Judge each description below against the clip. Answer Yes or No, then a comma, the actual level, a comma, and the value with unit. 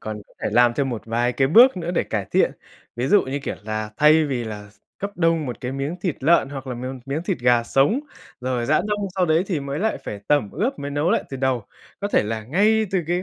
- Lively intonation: Yes, wide, 6.0 semitones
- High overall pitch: No, medium, 140 Hz